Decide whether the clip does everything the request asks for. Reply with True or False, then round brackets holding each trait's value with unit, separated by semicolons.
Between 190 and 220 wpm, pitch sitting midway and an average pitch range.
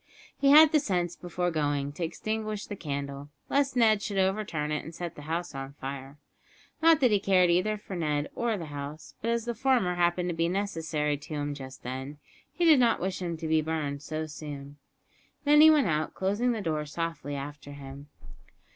False (200 wpm; 165 Hz; 6.1 semitones)